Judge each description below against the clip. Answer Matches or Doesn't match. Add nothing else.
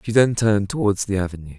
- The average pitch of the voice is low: Matches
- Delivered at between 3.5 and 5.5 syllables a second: Doesn't match